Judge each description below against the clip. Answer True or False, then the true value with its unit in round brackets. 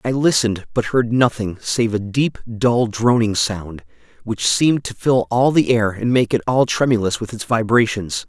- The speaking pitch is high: False (115 Hz)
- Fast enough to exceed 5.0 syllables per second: False (4.7 syllables/s)